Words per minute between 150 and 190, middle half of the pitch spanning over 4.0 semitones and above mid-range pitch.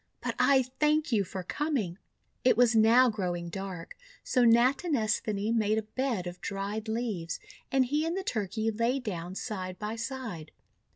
Yes: average, 160 wpm; average, 4.5 semitones; high, 220 Hz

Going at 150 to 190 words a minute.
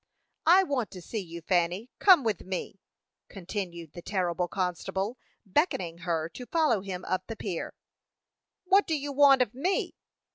Yes: average, 155 wpm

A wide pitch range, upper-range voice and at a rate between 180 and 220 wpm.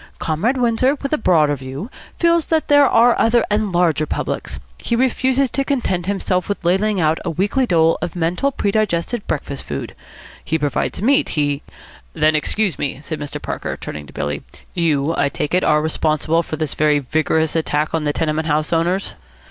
No: wide, 6.2 semitones; medium, 170 Hz; average, 190 wpm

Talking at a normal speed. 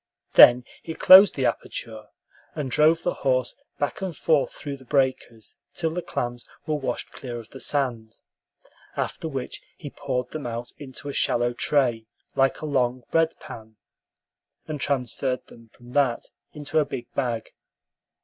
Yes: average, 160 wpm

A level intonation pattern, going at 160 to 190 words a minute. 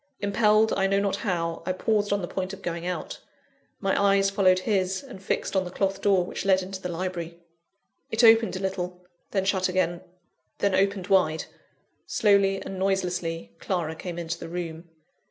Yes: narrow, 1.9 semitones; average, 180 wpm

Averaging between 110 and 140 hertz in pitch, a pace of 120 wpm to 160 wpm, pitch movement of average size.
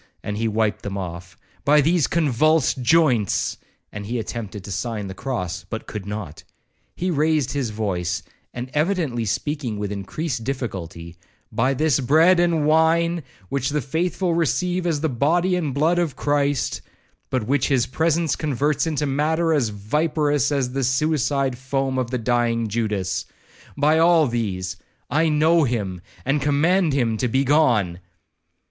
No: low, 135 Hz; average, 145 wpm; wide, 6.0 semitones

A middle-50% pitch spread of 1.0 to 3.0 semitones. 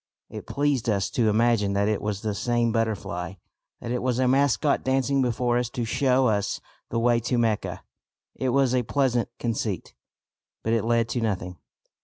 Yes: average, 2.7 semitones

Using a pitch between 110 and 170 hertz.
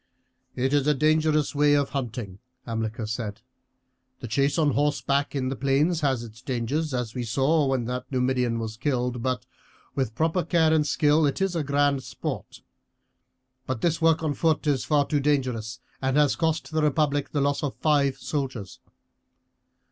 Yes: medium, 140 Hz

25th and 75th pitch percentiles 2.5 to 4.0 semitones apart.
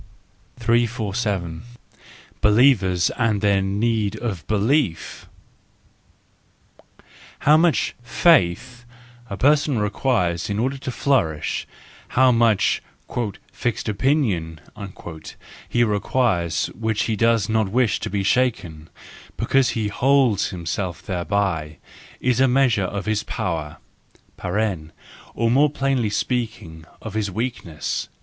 No: average, 4.7 semitones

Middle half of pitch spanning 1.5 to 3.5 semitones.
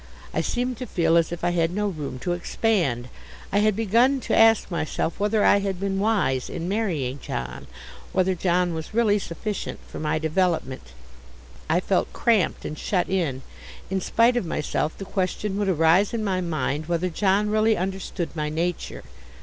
No: average, 4.3 semitones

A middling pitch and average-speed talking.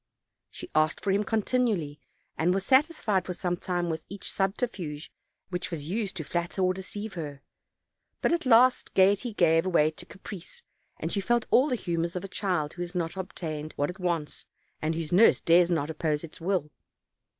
Yes: medium, 180 Hz; average, 185 wpm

